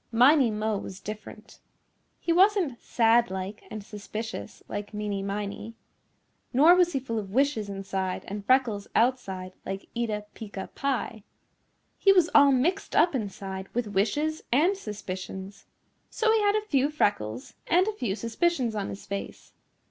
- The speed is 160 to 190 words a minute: No, average, 150 wpm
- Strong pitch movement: Yes, wide, 6.1 semitones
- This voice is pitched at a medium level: No, high, 220 Hz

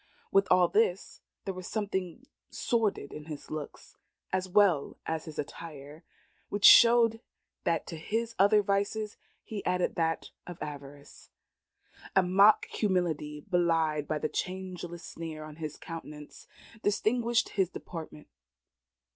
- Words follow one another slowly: Yes, slow, 130 wpm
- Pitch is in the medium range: Yes, medium, 180 Hz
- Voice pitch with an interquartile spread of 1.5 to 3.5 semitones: No, average, 4.6 semitones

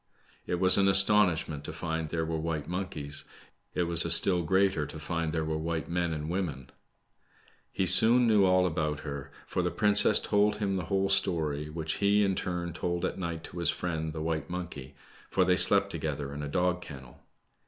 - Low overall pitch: Yes, very low, 85 Hz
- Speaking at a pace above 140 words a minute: Yes, average, 200 wpm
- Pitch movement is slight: No, average, 3.3 semitones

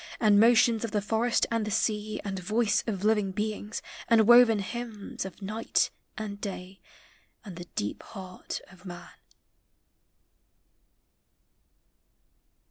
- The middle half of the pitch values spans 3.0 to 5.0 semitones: No, narrow, 2.5 semitones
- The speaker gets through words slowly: Yes, slow, 125 wpm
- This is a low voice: No, high, 210 Hz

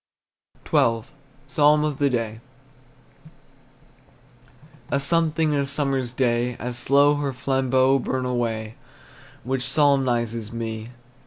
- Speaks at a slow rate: Yes, slow, 105 wpm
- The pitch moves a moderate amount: Yes, average, 3.1 semitones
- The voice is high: No, low, 130 Hz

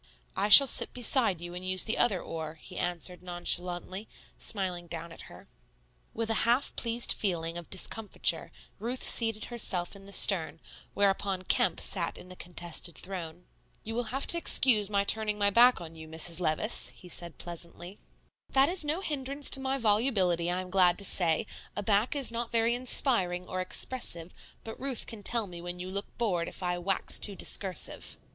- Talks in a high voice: Yes, high, 195 Hz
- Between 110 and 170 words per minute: No, average, 185 wpm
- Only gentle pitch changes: No, average, 4.6 semitones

